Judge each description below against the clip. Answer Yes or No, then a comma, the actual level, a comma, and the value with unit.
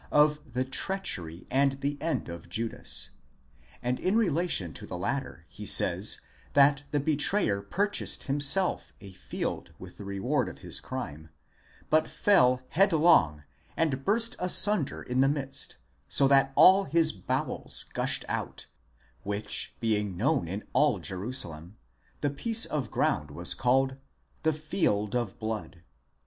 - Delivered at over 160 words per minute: No, average, 145 wpm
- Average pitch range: No, wide, 7.3 semitones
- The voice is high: No, low, 135 Hz